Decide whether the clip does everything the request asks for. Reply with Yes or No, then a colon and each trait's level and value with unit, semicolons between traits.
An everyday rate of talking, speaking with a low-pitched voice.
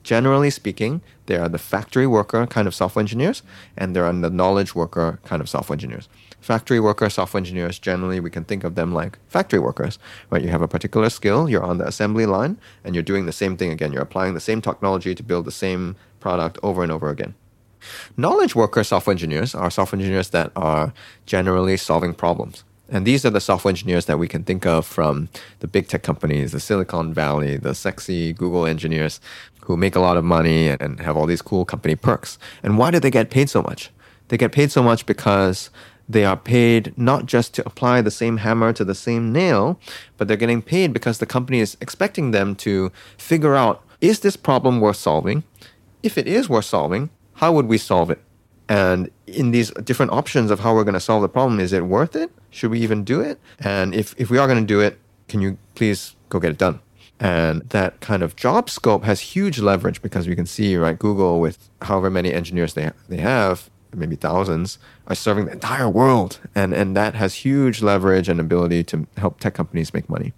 No: fast, 215 wpm; low, 100 Hz